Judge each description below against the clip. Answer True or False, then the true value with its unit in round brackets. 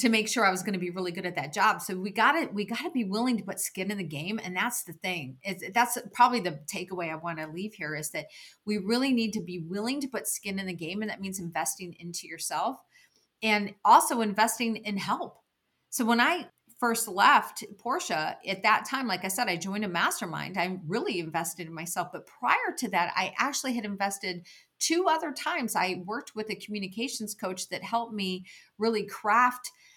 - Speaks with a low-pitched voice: False (205 Hz)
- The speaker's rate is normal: False (220 wpm)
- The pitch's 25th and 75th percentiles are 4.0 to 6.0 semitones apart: True (4.4 semitones)